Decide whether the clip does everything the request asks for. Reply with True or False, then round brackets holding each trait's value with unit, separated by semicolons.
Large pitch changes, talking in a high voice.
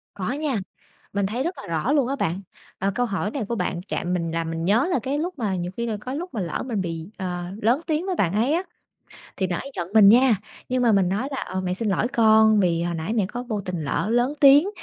True (5.9 semitones; 215 Hz)